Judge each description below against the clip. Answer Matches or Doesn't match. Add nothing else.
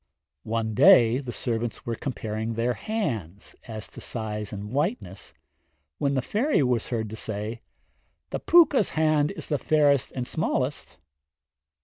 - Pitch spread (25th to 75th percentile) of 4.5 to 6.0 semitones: Matches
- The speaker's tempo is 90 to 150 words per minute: Matches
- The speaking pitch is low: Matches